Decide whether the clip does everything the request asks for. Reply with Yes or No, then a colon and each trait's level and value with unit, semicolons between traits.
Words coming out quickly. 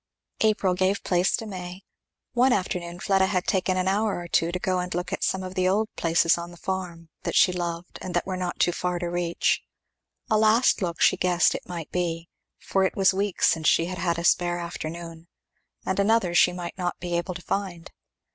Yes: fast, 215 wpm